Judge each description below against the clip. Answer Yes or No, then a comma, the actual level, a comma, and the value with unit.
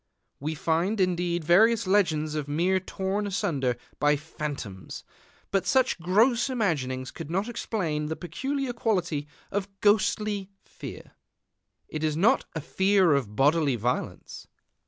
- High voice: No, medium, 175 Hz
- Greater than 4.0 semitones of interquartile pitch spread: Yes, average, 5.3 semitones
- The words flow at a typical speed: No, slow, 130 wpm